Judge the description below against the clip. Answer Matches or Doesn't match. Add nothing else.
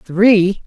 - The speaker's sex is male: Doesn't match